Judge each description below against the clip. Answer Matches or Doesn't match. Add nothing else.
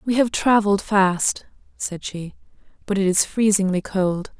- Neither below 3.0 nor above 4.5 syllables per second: Matches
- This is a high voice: Matches